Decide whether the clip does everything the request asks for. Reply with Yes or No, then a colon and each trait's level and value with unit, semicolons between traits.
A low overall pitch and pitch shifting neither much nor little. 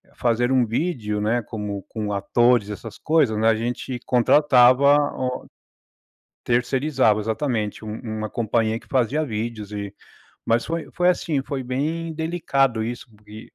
Yes: low, 120 Hz; average, 3.9 semitones